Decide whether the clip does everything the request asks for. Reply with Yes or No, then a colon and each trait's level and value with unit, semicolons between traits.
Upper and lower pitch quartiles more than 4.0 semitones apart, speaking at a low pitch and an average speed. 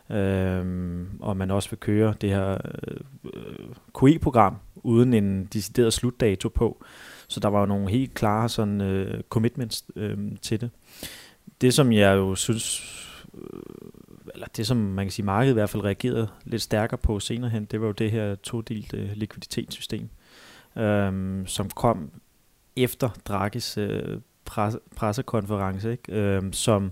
No: average, 2.8 semitones; low, 105 Hz; average, 155 wpm